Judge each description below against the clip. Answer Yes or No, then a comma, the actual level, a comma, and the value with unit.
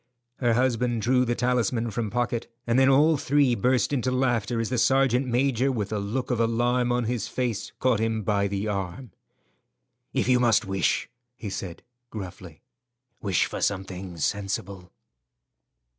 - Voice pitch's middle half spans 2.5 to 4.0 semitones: Yes, average, 3.7 semitones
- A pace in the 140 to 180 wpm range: Yes, average, 160 wpm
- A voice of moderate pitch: No, low, 120 Hz